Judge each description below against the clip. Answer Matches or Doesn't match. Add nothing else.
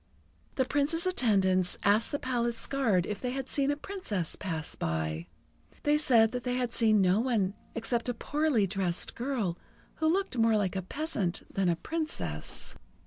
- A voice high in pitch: Matches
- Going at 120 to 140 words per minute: Doesn't match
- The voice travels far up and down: Matches